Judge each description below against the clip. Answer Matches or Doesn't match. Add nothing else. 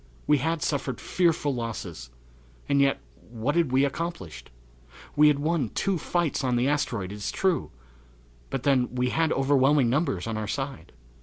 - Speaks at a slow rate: Doesn't match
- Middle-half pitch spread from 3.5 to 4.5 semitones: Matches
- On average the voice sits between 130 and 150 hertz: Matches